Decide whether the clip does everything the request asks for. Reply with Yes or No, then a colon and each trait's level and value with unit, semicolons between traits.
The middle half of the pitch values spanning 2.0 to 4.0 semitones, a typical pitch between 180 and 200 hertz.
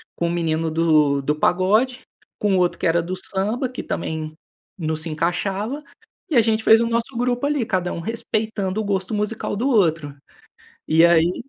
No: average, 5.2 semitones; high, 190 Hz